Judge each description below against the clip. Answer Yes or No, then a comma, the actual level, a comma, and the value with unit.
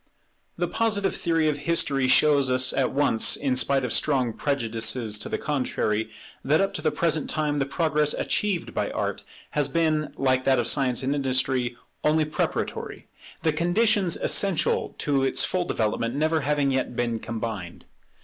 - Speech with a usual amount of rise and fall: Yes, average, 3.6 semitones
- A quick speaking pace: No, average, 165 wpm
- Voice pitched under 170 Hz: Yes, medium, 140 Hz